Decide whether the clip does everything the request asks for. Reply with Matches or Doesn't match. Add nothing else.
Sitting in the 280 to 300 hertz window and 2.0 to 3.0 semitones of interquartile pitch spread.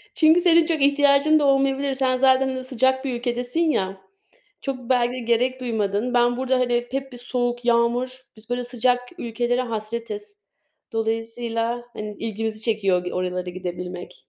Doesn't match